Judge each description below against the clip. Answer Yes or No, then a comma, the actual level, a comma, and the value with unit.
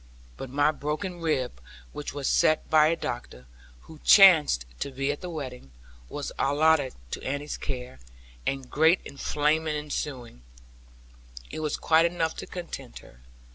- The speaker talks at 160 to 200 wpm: No, average, 145 wpm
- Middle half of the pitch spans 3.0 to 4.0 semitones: Yes, average, 3.3 semitones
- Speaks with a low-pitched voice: No, medium, 150 Hz